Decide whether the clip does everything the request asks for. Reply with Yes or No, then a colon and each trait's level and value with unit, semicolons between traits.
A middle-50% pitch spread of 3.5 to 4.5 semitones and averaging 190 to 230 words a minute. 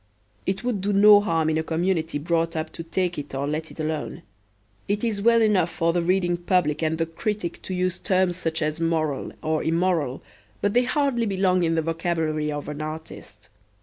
No: average, 3.1 semitones; average, 200 wpm